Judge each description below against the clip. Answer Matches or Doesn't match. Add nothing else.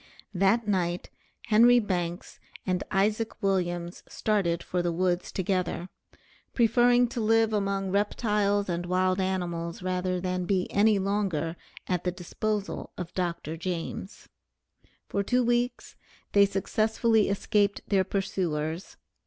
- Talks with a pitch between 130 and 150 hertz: Doesn't match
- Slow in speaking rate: Matches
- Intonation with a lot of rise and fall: Doesn't match